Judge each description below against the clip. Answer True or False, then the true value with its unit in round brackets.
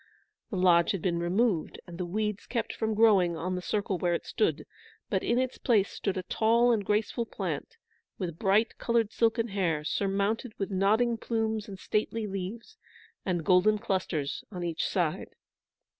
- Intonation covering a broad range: False (3.7 semitones)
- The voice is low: False (200 Hz)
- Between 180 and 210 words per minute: False (170 wpm)